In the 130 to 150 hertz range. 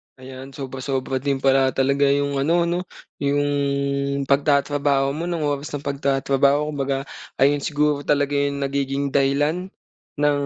Yes: medium, 140 Hz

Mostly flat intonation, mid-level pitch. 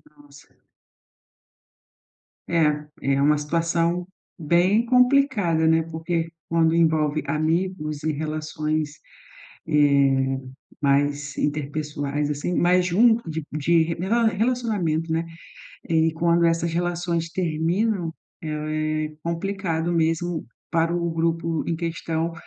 Yes: narrow, 2.2 semitones; medium, 165 Hz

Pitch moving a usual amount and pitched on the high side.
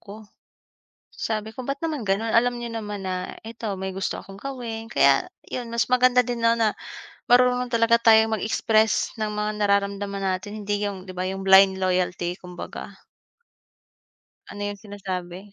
Yes: average, 3.1 semitones; high, 210 Hz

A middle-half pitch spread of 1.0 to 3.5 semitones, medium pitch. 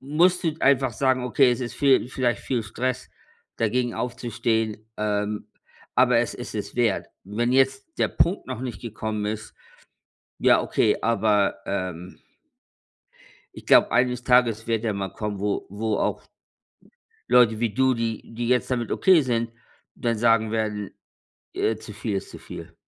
No: average, 2.9 semitones; low, 115 Hz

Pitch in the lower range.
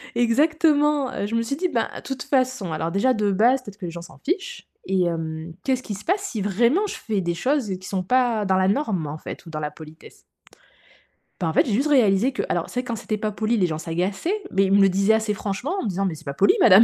No: high, 210 Hz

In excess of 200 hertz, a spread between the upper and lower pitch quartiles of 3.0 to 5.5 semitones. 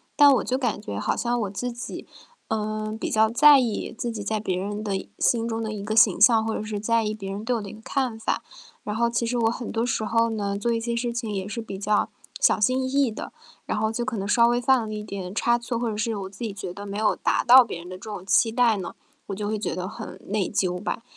No: high, 220 Hz; narrow, 2.5 semitones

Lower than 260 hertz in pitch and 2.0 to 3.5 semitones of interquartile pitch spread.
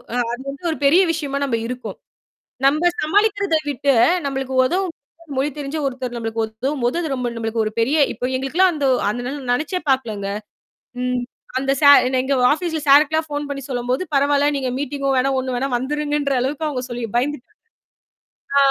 No: very high, 275 Hz; average, 2.9 semitones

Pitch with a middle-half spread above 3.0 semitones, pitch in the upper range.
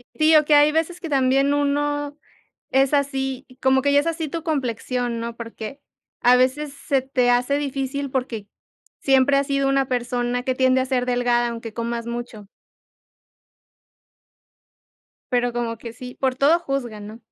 No: average, 2.7 semitones; very high, 265 Hz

